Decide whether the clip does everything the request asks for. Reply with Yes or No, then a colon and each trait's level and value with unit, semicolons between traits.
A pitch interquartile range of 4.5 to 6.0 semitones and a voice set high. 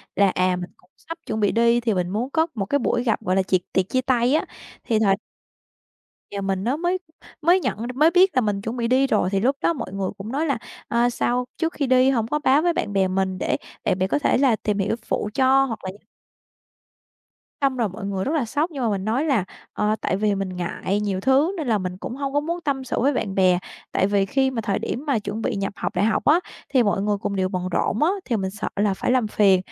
Yes: wide, 5.6 semitones; high, 225 Hz